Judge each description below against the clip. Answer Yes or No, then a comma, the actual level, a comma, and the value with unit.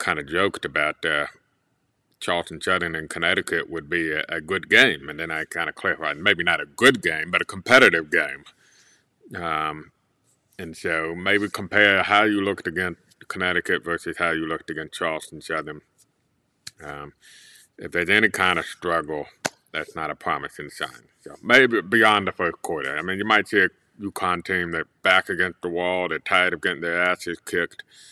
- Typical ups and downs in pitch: Yes, average, 3.3 semitones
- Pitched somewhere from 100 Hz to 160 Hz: No, very low, 85 Hz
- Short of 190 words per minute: Yes, average, 180 wpm